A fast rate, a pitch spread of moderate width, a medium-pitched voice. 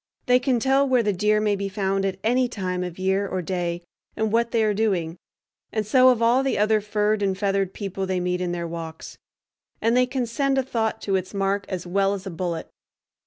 No: fast, 225 wpm; average, 3.6 semitones; high, 200 Hz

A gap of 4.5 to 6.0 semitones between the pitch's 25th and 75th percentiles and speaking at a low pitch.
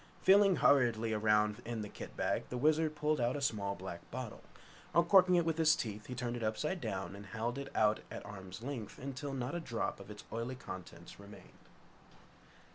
Yes: wide, 5.6 semitones; low, 120 Hz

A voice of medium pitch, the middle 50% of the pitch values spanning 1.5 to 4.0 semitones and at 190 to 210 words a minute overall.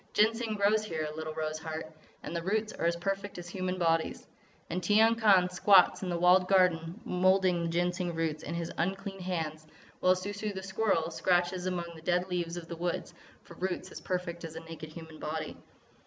Yes: medium, 180 Hz; narrow, 2.5 semitones; average, 200 wpm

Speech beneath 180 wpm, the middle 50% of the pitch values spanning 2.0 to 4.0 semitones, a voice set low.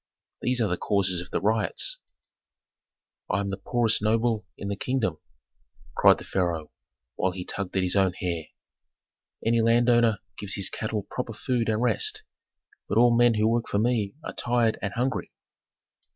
Yes: average, 165 wpm; average, 3.4 semitones; low, 110 Hz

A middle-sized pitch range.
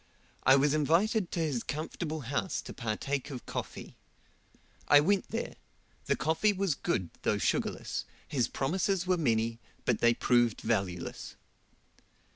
No: wide, 6.3 semitones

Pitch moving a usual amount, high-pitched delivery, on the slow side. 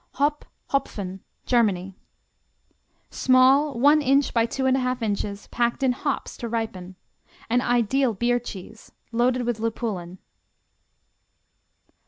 Yes: average, 3.4 semitones; high, 240 Hz; slow, 110 wpm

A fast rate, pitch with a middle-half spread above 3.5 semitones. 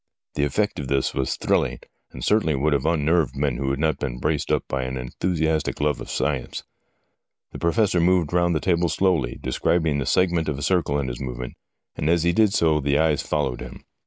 Yes: fast, 210 wpm; average, 3.9 semitones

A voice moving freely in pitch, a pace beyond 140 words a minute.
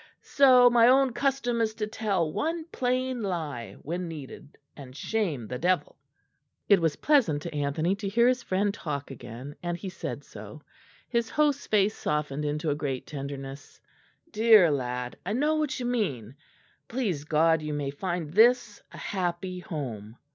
Yes: wide, 8.1 semitones; average, 160 wpm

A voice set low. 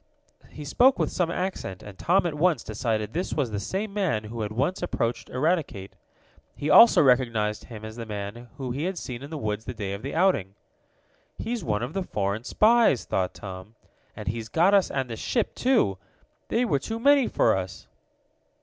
Yes: low, 125 Hz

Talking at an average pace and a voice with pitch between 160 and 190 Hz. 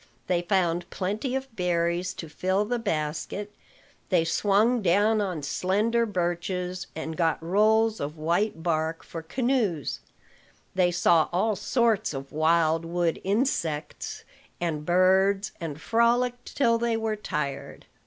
No: slow, 130 wpm; medium, 185 Hz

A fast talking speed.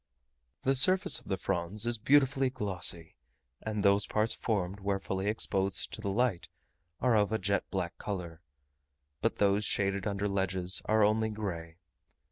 No: average, 155 wpm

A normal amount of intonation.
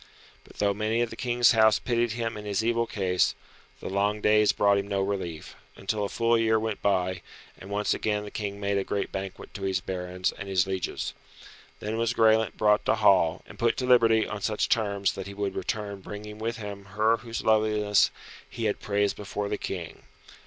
No: narrow, 2.1 semitones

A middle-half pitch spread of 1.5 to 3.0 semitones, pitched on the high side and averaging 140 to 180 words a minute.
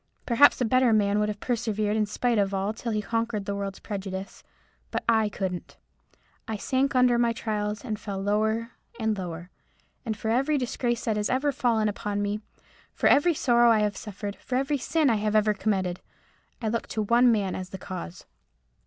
No: average, 2.7 semitones; high, 215 Hz; average, 190 wpm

